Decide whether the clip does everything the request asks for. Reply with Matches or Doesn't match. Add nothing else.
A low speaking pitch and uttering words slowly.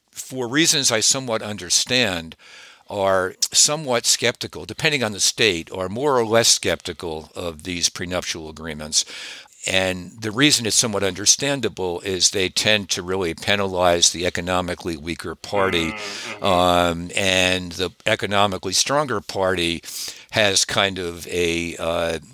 Matches